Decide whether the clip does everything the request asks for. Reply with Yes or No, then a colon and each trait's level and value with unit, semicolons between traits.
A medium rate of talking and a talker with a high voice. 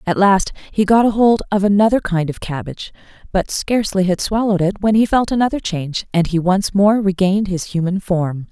Yes: average, 195 wpm; high, 195 Hz